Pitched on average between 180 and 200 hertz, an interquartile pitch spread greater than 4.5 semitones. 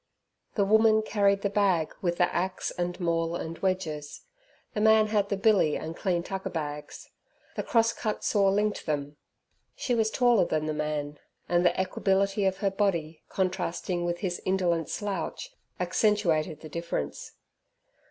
No: medium, 185 Hz; average, 3.8 semitones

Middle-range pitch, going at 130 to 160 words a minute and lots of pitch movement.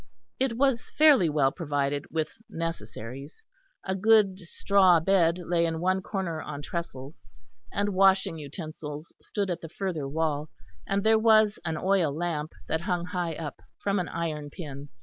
No: medium, 170 Hz; average, 155 wpm; average, 4.3 semitones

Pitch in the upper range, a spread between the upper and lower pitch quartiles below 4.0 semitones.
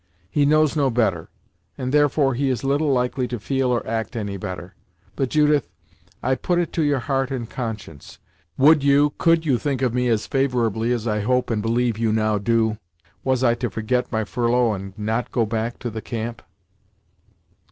No: low, 125 Hz; average, 3.4 semitones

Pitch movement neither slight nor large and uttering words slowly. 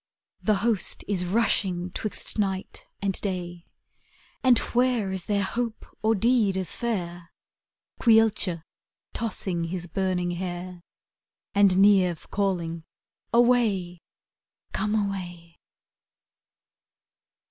Yes: average, 3.5 semitones; slow, 100 wpm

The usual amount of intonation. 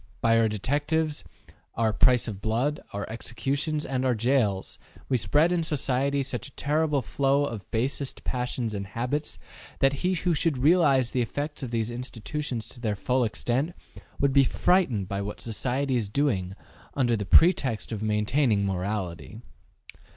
Yes: average, 4.6 semitones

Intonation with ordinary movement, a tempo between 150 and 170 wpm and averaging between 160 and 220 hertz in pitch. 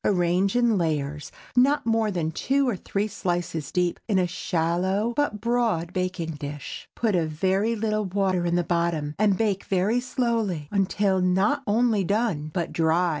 Yes: average, 4.2 semitones; average, 155 wpm; high, 190 Hz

